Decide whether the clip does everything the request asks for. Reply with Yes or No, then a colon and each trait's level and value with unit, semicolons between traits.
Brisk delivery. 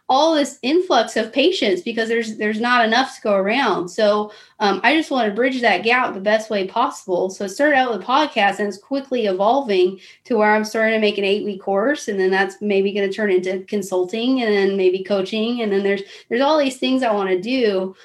Yes: fast, 235 wpm